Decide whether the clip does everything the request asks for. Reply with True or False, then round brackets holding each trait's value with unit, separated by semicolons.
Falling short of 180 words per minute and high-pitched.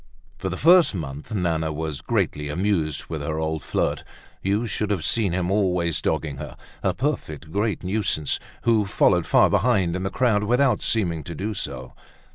False (170 wpm; 90 Hz)